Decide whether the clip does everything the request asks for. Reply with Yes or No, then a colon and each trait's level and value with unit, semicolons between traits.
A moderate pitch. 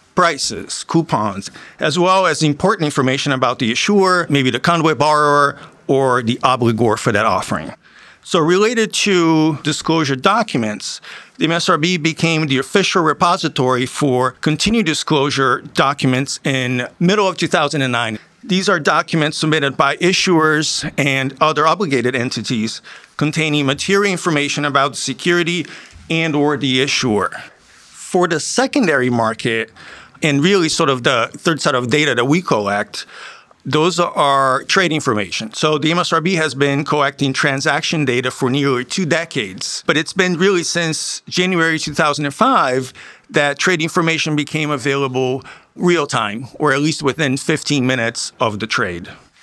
Yes: medium, 150 Hz